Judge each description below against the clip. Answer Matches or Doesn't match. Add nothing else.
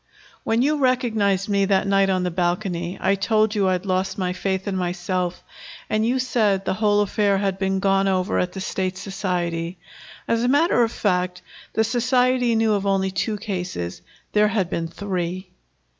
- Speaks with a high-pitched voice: Matches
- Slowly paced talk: Doesn't match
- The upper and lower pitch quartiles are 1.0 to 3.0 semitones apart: Matches